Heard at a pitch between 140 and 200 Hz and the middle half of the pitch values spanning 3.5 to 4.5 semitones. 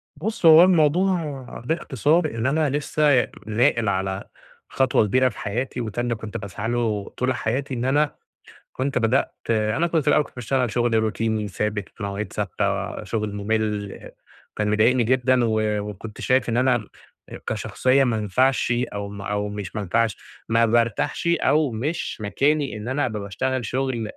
No: low, 120 Hz; average, 4.0 semitones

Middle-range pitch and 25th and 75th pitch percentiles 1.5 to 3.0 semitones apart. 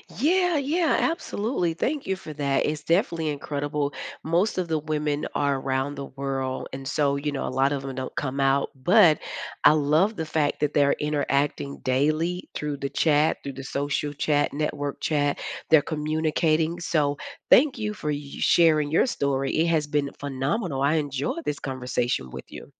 Yes: medium, 150 Hz; narrow, 2.5 semitones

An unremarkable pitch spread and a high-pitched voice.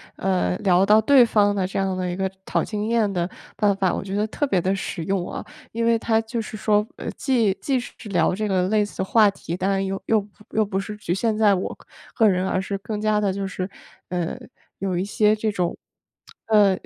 No: narrow, 2.3 semitones; high, 200 Hz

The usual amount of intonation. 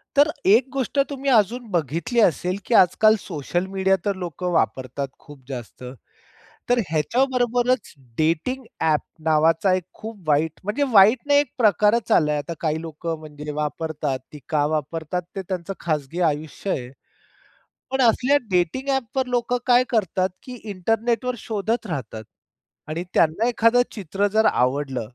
No: wide, 7.3 semitones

